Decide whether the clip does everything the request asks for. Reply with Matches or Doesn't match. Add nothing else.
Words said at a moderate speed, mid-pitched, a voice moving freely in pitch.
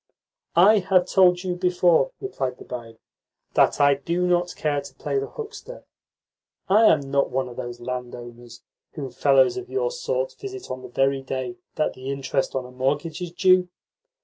Matches